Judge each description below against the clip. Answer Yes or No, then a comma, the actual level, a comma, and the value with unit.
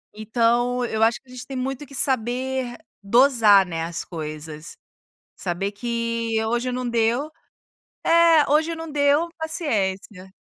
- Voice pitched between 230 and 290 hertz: Yes, high, 240 Hz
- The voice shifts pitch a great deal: No, average, 4.7 semitones